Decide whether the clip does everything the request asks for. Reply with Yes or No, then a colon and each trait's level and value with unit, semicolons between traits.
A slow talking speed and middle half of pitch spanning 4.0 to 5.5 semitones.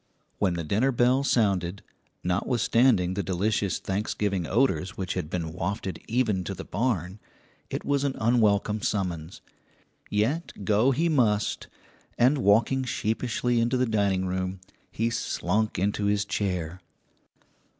Yes: slow, 130 wpm; average, 4.3 semitones